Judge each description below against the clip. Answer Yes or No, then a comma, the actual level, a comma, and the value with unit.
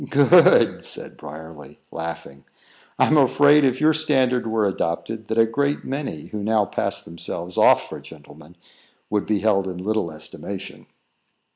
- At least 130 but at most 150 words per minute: Yes, average, 145 wpm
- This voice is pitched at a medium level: No, low, 105 Hz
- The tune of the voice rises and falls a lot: Yes, wide, 7.9 semitones